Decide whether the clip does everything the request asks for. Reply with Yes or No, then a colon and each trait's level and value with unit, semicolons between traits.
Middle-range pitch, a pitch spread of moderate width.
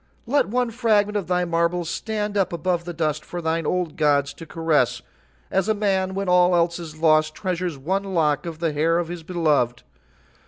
Yes: medium, 170 Hz; average, 3.1 semitones